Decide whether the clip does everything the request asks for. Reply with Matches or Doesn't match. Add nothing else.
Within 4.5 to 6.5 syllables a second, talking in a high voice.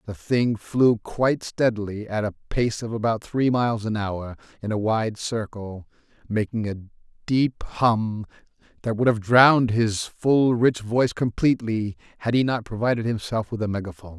Doesn't match